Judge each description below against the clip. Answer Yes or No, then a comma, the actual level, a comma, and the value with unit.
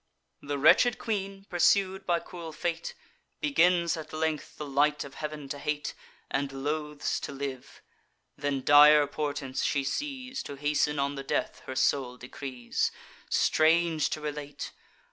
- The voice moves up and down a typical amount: Yes, average, 3.2 semitones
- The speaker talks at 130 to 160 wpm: Yes, average, 145 wpm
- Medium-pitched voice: Yes, medium, 150 Hz